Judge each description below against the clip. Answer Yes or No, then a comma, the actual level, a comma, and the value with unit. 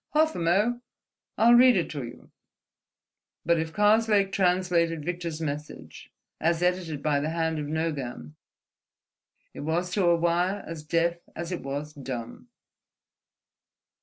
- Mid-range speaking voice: Yes, medium, 170 Hz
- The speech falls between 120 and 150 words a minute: Yes, average, 140 wpm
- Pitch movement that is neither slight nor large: Yes, average, 3.2 semitones